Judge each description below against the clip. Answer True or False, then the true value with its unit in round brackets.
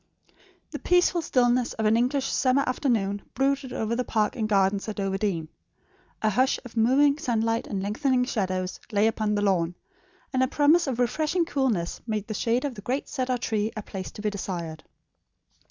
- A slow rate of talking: False (180 wpm)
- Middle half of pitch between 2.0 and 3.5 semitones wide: False (4.3 semitones)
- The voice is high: True (225 Hz)